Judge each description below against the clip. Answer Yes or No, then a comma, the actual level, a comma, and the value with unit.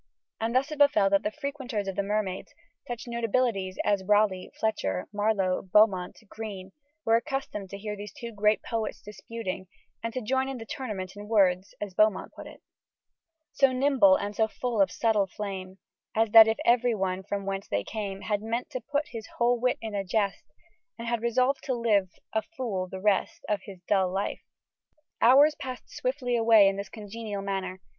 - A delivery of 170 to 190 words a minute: Yes, average, 180 wpm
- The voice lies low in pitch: No, high, 215 Hz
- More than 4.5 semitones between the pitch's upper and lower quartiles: No, average, 3.2 semitones